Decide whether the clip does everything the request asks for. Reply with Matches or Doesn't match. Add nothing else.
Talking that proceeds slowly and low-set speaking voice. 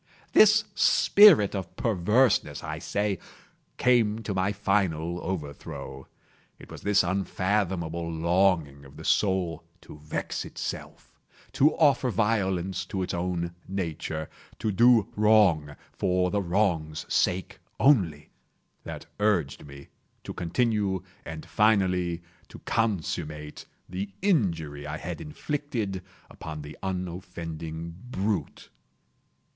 Matches